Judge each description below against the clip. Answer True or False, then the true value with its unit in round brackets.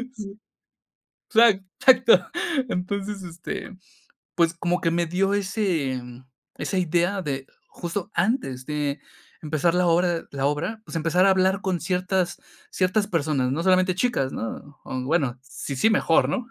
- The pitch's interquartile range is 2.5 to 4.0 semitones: False (4.4 semitones)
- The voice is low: False (175 Hz)